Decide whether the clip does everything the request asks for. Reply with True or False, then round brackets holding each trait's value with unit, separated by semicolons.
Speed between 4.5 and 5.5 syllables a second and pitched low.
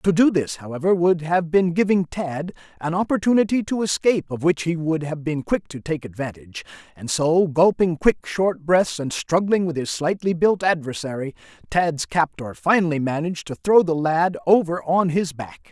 False (4.9 syllables/s; 165 Hz)